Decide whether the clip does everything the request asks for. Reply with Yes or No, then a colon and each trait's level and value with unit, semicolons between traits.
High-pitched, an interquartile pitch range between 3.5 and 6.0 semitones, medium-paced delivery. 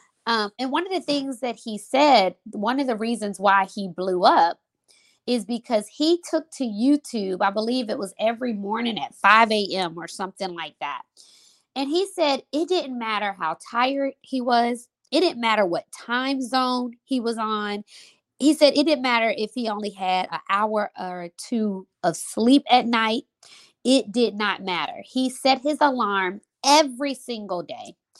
Yes: high, 235 Hz; average, 4.6 semitones; average, 175 wpm